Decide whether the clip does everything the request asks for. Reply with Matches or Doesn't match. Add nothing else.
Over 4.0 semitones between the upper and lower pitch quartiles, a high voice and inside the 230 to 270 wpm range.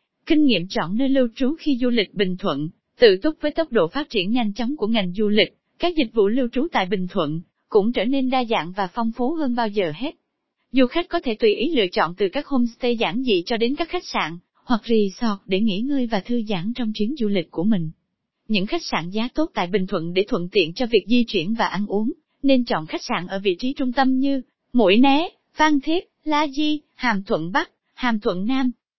Matches